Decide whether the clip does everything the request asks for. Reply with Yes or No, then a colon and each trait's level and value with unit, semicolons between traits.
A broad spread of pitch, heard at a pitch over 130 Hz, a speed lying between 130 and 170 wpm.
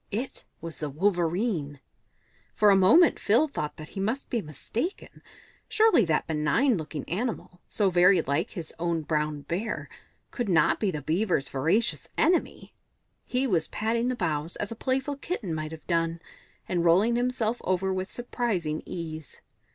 Yes: wide, 6.6 semitones; medium, 185 Hz; average, 160 wpm